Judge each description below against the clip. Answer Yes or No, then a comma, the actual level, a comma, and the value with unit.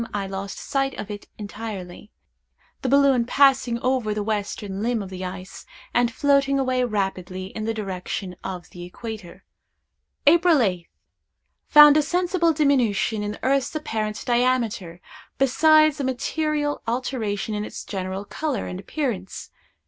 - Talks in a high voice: Yes, high, 225 Hz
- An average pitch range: No, wide, 5.8 semitones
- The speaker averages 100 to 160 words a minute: Yes, average, 140 wpm